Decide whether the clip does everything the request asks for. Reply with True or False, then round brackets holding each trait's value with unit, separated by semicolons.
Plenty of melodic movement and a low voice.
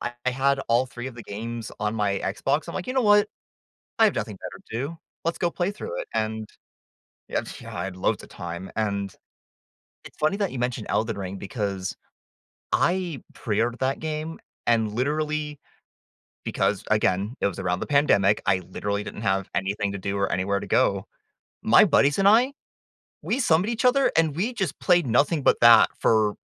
True (8.2 semitones; 120 Hz)